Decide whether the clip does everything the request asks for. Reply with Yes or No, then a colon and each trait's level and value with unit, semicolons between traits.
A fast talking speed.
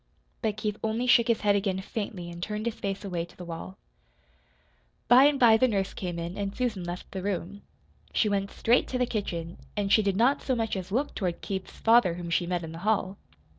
Yes: fast, 225 wpm